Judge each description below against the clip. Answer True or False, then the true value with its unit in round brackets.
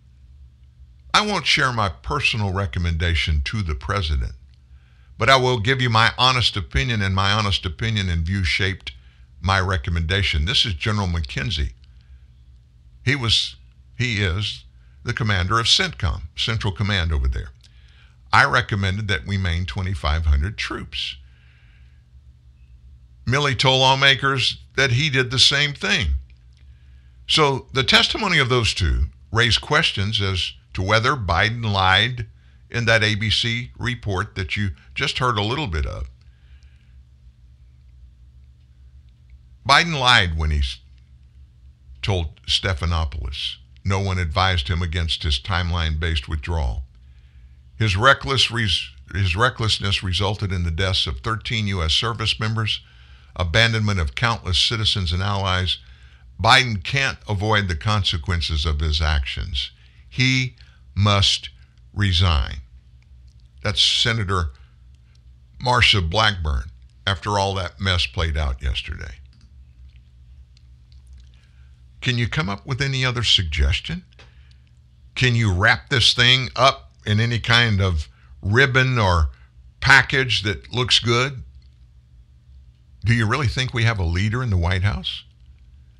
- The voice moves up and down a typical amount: False (9.0 semitones)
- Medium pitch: False (85 Hz)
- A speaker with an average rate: False (125 wpm)